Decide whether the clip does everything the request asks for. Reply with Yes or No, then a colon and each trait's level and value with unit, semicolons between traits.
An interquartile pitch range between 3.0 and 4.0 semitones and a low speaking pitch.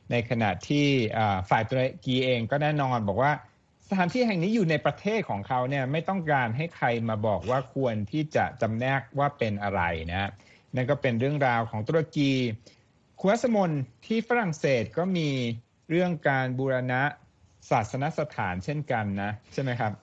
No: average, 4.7 semitones; low, 130 Hz